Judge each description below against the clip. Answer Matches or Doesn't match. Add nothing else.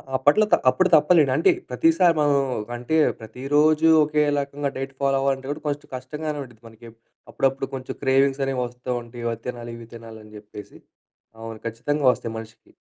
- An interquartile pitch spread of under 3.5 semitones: Doesn't match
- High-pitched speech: Doesn't match